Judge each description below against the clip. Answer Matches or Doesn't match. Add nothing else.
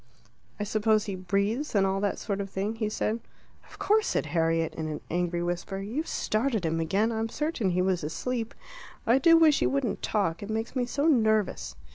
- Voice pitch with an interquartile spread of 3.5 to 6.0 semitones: Matches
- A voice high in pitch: Matches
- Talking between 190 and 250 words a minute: Matches